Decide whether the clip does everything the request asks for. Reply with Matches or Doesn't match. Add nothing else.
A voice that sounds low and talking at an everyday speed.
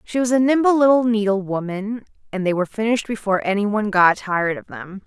Doesn't match